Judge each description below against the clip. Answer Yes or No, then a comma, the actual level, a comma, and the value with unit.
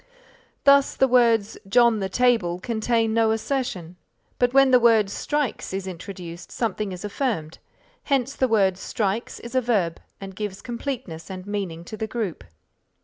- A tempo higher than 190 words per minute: No, average, 155 wpm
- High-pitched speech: Yes, high, 220 Hz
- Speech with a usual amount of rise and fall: Yes, average, 4.4 semitones